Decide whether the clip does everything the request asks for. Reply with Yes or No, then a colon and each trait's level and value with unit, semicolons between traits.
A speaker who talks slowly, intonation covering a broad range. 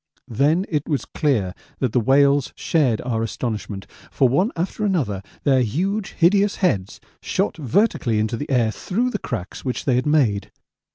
No: average, 165 wpm; wide, 6.8 semitones